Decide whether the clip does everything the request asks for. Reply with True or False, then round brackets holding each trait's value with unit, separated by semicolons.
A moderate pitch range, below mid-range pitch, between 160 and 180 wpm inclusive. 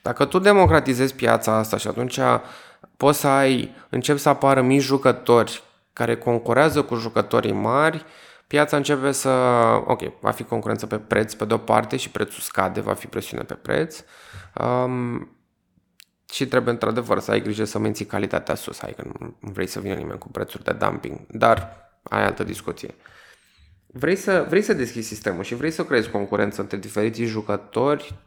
True (4.4 semitones; 120 Hz; 170 wpm)